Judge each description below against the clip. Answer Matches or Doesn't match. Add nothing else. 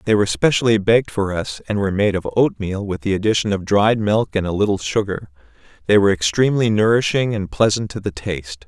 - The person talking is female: Doesn't match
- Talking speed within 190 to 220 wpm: Matches